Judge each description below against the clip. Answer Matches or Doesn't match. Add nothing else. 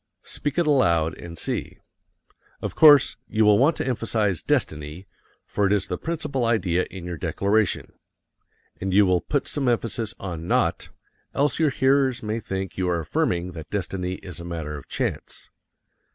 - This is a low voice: Matches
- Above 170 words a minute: Doesn't match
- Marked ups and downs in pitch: Matches